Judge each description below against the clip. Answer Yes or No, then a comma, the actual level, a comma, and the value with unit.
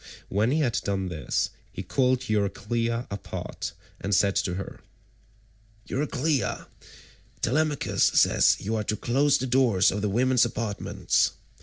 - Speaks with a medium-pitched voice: No, low, 115 Hz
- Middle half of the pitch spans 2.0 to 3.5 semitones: No, average, 4.3 semitones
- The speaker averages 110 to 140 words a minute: Yes, slow, 135 wpm